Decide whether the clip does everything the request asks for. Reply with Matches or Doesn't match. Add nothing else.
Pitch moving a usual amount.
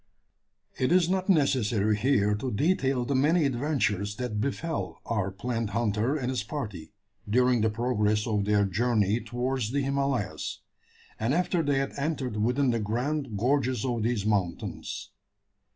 Matches